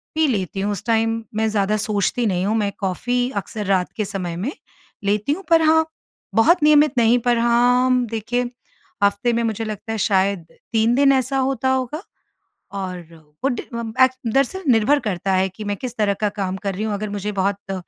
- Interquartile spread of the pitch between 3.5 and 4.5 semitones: Yes, average, 3.8 semitones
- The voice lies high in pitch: Yes, high, 220 Hz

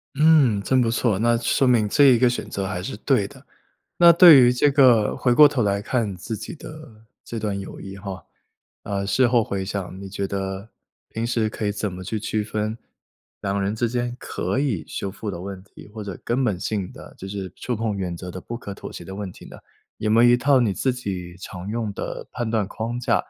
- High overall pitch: No, low, 110 Hz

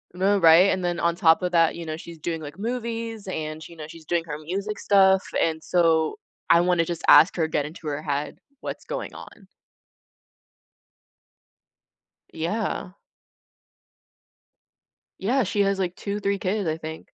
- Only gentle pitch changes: No, average, 3.7 semitones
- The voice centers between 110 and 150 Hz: No, medium, 170 Hz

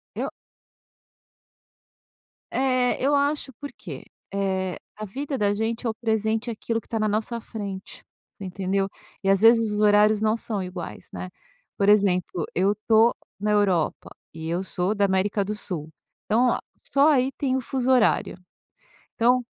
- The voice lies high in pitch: Yes, high, 215 Hz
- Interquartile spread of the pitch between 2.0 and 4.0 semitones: Yes, average, 3.4 semitones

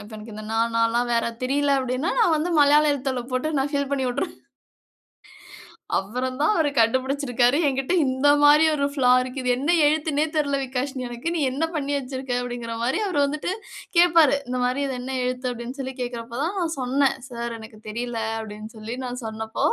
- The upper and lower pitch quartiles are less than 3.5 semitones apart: Yes, average, 3.0 semitones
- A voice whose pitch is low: No, very high, 260 Hz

